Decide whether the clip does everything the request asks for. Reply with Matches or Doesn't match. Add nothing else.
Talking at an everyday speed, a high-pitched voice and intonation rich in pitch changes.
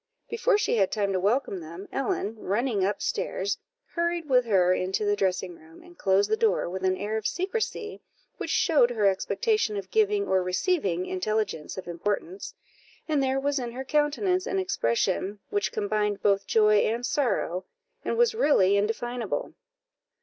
Matches